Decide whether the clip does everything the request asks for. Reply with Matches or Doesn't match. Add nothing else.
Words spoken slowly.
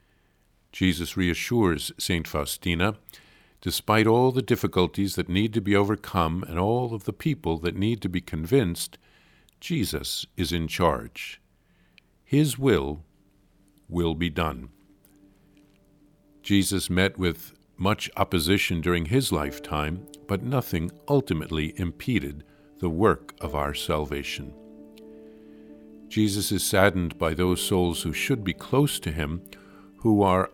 Matches